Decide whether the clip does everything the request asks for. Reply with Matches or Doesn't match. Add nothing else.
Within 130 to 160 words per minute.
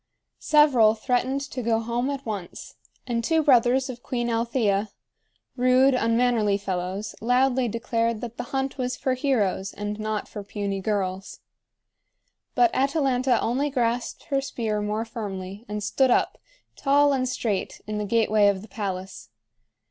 Matches